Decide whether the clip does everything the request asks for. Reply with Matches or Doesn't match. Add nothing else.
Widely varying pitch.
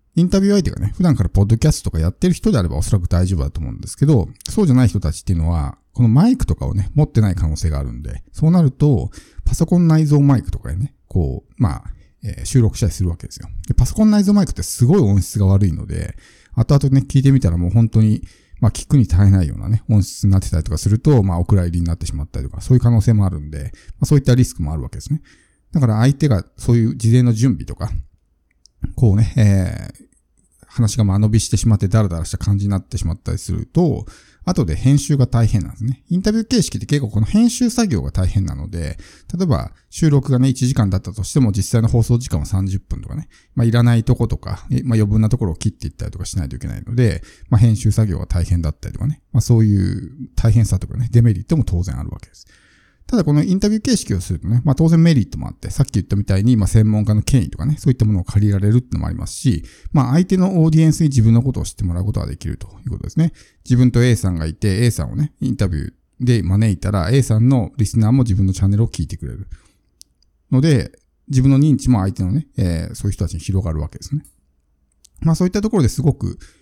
Matches